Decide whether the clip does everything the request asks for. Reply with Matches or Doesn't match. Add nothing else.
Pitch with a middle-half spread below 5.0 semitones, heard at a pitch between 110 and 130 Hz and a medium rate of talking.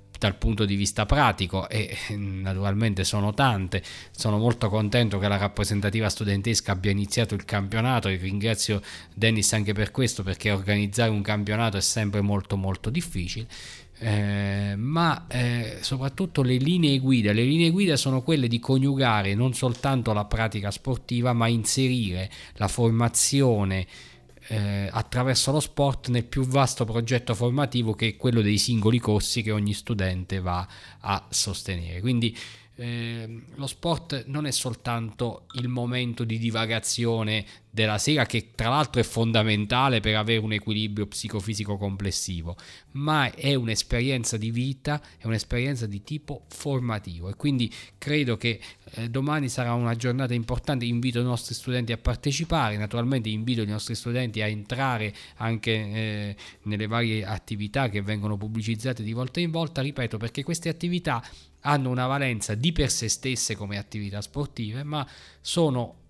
Matches